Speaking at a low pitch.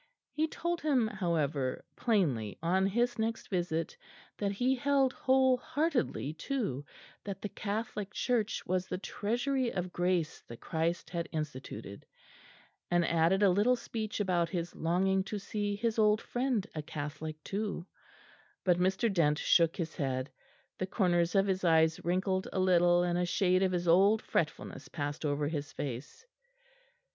No: medium, 185 Hz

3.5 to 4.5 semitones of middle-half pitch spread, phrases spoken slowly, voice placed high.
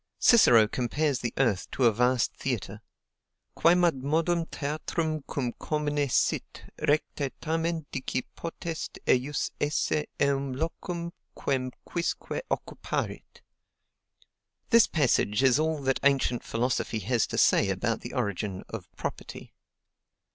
No: average, 4.2 semitones; slow, 115 wpm; medium, 140 Hz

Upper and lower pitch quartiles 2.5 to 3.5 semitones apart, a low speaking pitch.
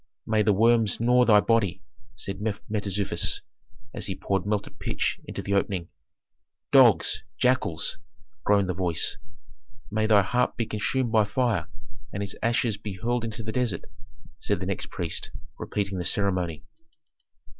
Yes: average, 2.9 semitones; low, 105 Hz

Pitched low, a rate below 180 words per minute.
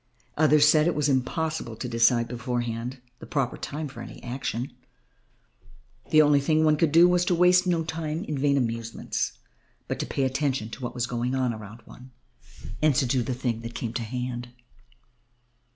No: low, 130 Hz; average, 185 wpm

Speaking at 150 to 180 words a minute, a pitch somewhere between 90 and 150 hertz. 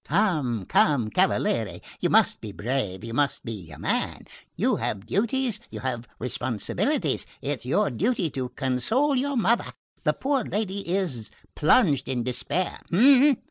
No: average, 140 wpm; medium, 140 Hz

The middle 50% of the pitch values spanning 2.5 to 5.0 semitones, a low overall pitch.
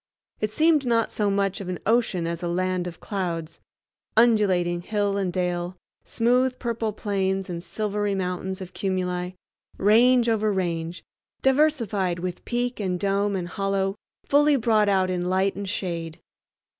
No: average, 3.4 semitones; high, 195 Hz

